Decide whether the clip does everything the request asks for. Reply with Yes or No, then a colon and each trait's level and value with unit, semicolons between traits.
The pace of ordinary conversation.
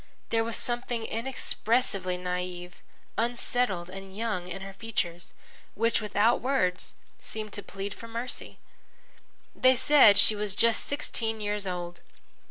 No: slow, 130 wpm